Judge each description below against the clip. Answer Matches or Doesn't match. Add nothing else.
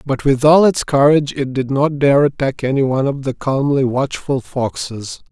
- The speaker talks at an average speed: Matches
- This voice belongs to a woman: Doesn't match